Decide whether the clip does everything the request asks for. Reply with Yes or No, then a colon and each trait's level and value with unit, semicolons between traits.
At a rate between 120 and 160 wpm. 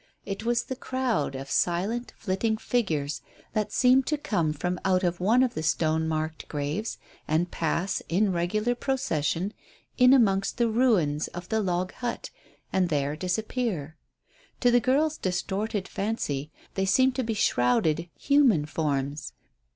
Yes: average, 150 wpm